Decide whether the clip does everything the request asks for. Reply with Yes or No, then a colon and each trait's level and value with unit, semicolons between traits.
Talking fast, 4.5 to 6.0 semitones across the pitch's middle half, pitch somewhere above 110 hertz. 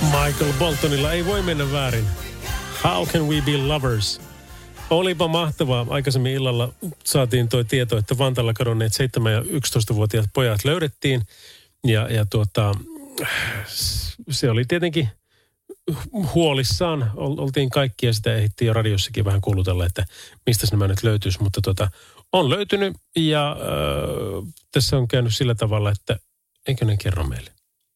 No: average, 135 wpm; average, 5.2 semitones; low, 120 Hz